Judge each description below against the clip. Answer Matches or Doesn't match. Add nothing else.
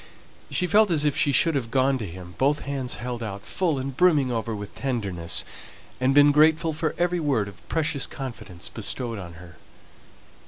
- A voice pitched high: Doesn't match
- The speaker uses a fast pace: Doesn't match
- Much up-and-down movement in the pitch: Matches